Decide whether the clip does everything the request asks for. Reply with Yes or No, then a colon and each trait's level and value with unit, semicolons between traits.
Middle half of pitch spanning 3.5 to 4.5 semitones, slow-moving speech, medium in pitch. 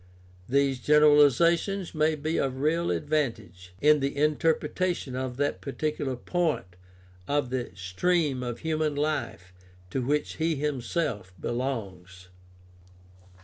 Yes: average, 4.0 semitones; slow, 110 wpm; medium, 145 Hz